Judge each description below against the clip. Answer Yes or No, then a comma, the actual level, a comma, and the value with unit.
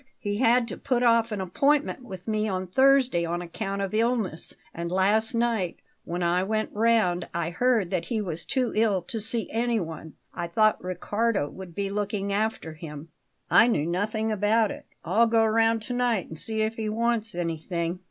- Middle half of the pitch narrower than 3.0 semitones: No, average, 4.3 semitones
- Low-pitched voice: No, high, 210 Hz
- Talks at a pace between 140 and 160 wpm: No, average, 185 wpm